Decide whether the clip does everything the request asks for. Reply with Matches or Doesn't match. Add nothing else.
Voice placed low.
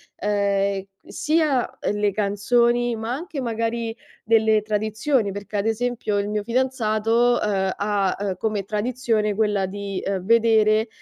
Doesn't match